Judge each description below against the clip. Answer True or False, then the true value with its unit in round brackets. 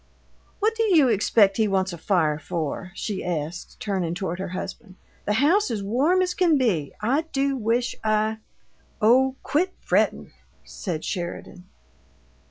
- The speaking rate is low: False (155 wpm)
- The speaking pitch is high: True (215 Hz)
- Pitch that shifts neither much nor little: False (6.8 semitones)